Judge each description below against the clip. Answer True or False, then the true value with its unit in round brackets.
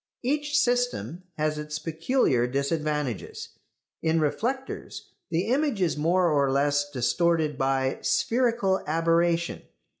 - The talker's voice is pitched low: False (165 Hz)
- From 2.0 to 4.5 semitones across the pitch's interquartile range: False (5.6 semitones)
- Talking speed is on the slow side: True (110 wpm)